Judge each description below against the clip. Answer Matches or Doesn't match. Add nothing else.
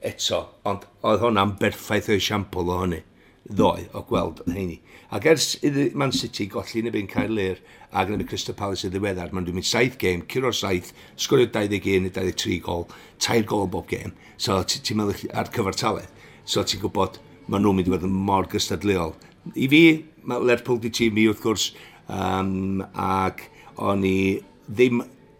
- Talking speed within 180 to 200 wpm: Matches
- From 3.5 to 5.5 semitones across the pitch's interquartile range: Doesn't match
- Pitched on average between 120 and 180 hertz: Doesn't match